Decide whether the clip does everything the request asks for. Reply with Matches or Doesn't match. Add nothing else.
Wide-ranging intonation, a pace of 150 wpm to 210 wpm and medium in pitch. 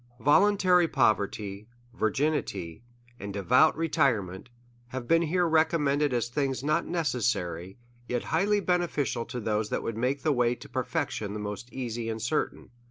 Doesn't match